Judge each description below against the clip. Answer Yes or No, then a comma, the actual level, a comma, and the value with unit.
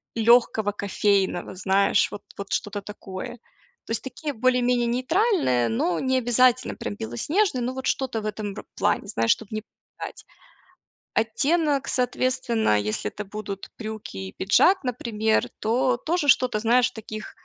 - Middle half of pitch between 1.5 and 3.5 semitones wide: No, average, 4.1 semitones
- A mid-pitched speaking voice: No, high, 225 Hz